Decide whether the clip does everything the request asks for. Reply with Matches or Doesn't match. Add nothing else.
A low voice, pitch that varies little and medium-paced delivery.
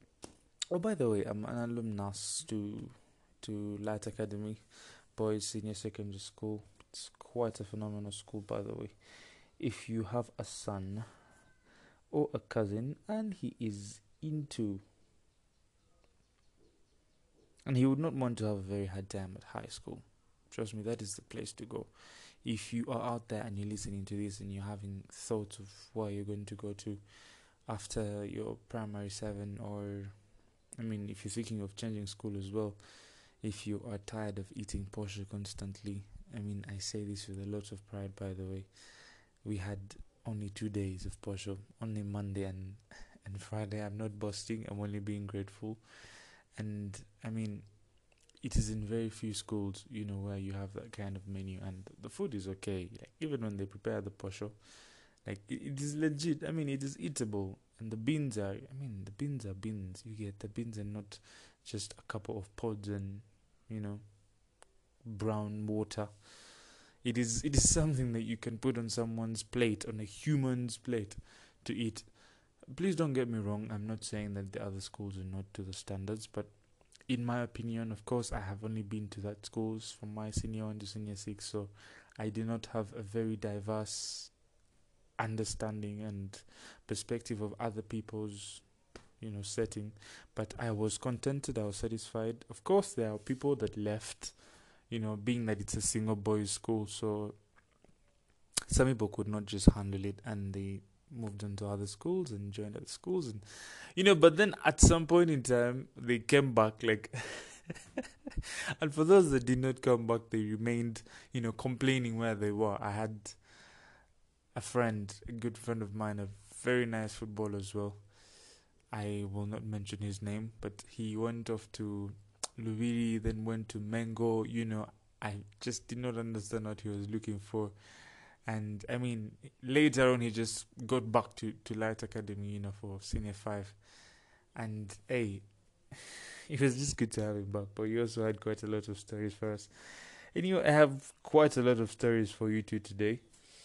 Matches